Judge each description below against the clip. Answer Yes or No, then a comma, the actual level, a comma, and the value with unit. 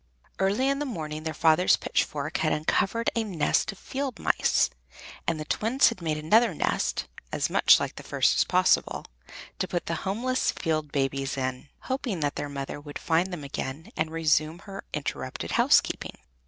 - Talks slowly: No, average, 175 wpm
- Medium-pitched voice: Yes, medium, 160 Hz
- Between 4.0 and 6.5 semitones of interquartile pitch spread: Yes, average, 5.2 semitones